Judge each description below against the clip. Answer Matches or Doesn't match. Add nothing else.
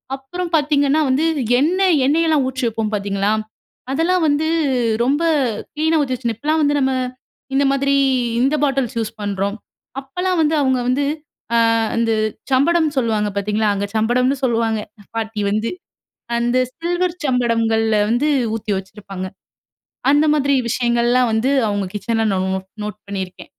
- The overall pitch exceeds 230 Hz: Matches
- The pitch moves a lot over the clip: Doesn't match